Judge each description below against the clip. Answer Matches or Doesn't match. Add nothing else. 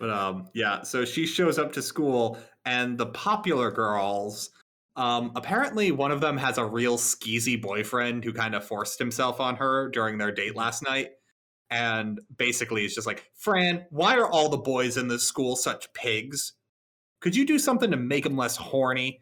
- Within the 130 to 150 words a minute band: Doesn't match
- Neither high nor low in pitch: Doesn't match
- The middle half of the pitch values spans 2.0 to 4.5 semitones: Matches